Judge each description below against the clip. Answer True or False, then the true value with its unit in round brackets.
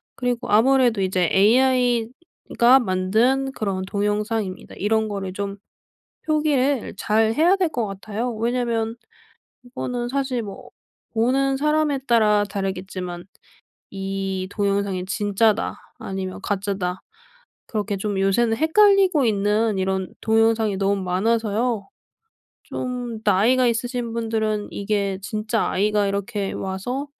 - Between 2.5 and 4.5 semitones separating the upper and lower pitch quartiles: True (3.8 semitones)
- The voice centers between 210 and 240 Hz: True (220 Hz)